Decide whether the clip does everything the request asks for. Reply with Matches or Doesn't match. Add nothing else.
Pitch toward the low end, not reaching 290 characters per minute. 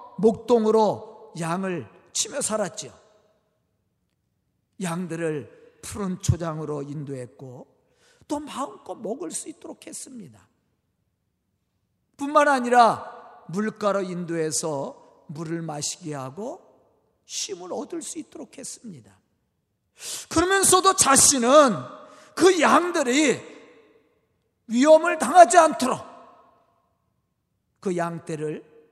Doesn't match